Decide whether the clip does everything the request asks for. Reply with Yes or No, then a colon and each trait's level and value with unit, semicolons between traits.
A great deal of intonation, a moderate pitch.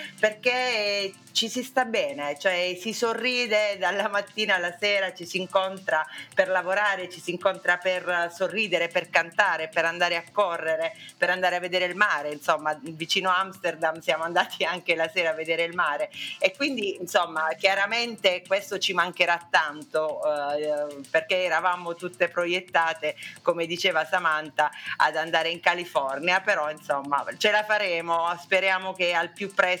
No: average, 3.0 semitones; medium, 180 Hz